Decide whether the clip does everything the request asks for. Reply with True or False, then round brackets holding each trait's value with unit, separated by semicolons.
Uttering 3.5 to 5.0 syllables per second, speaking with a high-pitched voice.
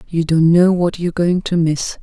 False (4.8 syllables/s; 170 Hz)